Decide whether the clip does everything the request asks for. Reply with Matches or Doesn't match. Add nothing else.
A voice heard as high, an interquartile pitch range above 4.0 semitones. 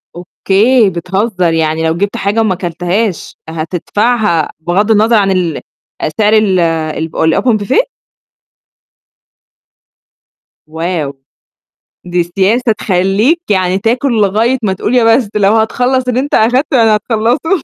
Matches